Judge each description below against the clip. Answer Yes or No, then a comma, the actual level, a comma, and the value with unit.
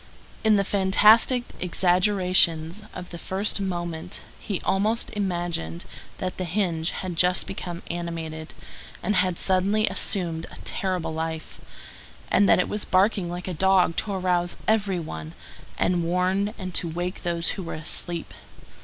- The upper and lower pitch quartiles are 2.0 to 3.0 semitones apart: Yes, narrow, 2.4 semitones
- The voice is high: No, medium, 180 Hz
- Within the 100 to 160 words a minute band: Yes, average, 145 wpm